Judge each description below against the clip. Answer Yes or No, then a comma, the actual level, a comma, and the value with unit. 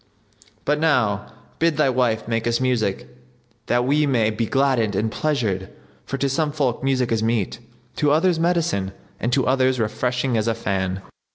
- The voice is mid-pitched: No, low, 125 Hz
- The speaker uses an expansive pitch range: No, average, 4.1 semitones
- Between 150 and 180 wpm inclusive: Yes, average, 170 wpm